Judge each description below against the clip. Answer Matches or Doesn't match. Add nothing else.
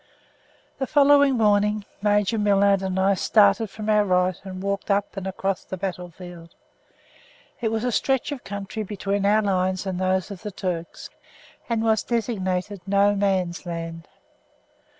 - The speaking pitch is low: Doesn't match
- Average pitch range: Doesn't match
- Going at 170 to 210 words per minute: Doesn't match